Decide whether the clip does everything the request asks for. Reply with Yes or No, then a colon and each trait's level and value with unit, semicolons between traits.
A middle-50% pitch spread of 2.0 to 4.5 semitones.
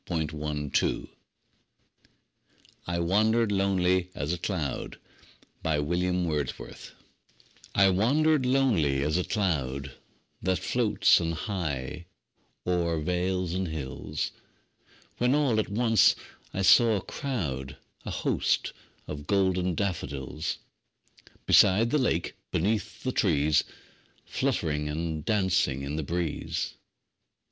No: average, 5.0 semitones